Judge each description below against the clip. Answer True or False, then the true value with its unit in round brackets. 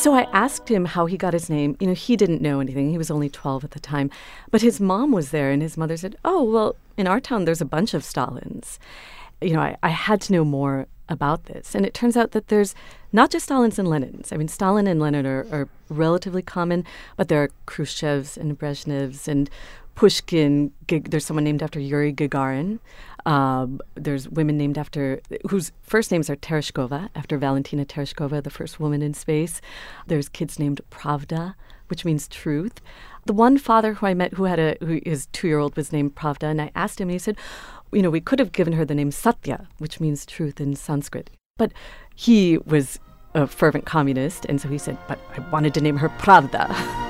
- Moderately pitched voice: True (155 Hz)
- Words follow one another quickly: True (210 wpm)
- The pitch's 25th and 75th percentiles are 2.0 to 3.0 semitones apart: False (4.7 semitones)